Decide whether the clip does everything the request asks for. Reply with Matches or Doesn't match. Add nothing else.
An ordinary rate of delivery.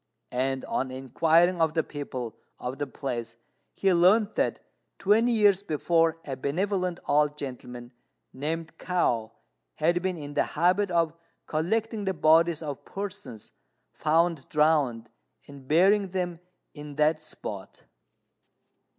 Doesn't match